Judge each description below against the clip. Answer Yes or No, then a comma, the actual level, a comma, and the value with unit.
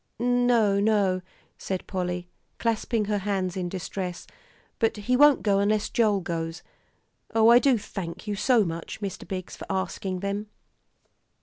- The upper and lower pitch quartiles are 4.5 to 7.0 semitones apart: No, average, 3.1 semitones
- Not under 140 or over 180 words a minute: Yes, average, 145 wpm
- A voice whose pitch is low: No, high, 200 Hz